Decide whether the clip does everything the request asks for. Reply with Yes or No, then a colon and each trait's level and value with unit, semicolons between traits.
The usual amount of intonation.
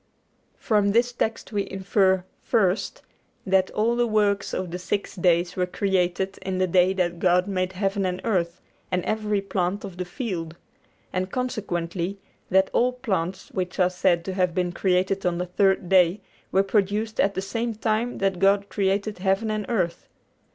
No: narrow, 2.3 semitones